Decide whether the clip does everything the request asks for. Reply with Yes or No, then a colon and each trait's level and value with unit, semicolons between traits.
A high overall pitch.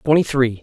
No: low, 135 Hz